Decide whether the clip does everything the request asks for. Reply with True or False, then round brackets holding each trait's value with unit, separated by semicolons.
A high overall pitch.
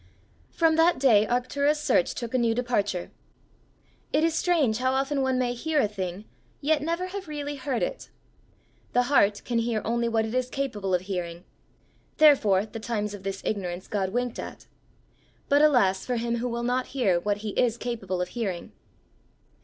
True (240 Hz)